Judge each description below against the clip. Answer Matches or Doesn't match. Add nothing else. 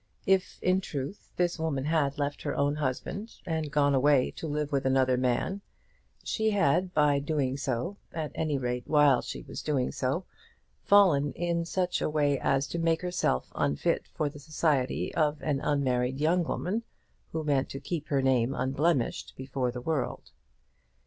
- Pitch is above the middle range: Doesn't match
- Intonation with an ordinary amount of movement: Matches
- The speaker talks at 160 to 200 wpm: Matches